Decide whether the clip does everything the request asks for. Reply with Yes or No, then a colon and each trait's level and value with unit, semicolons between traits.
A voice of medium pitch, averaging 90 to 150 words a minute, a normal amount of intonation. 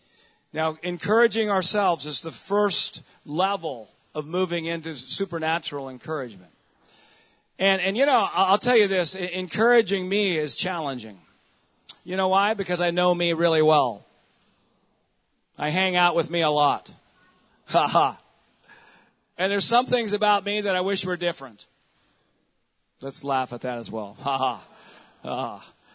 Yes: medium, 180 Hz; average, 140 wpm; average, 4.2 semitones